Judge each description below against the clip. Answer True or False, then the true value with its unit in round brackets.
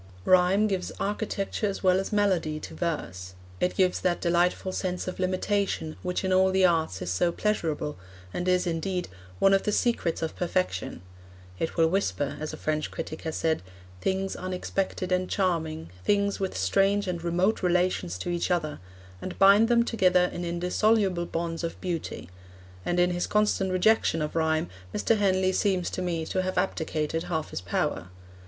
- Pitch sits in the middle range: True (180 Hz)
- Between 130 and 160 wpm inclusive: False (175 wpm)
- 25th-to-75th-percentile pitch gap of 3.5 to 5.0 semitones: False (2.8 semitones)